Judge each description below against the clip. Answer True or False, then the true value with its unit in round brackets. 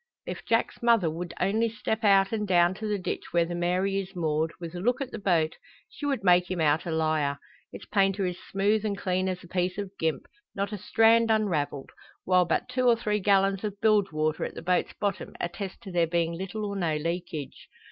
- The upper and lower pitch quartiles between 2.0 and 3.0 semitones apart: False (3.4 semitones)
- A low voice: False (185 Hz)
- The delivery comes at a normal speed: False (220 wpm)